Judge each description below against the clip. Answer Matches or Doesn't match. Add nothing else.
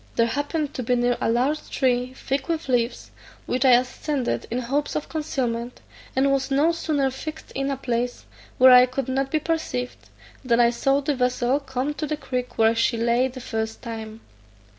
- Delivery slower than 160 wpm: Doesn't match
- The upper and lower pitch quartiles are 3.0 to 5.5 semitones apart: Doesn't match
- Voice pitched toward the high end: Matches